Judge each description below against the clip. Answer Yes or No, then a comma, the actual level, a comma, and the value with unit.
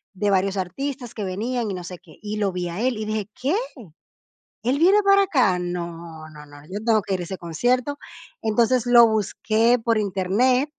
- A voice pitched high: Yes, high, 215 Hz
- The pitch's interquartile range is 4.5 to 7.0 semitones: Yes, average, 5.2 semitones